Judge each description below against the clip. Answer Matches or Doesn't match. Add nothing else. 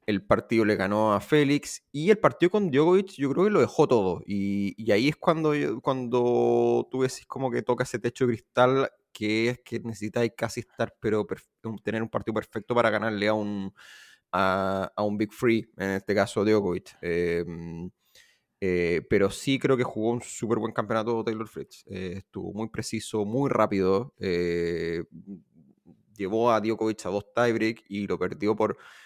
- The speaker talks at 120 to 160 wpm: Doesn't match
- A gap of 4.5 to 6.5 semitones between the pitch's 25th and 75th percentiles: Doesn't match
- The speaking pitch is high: Doesn't match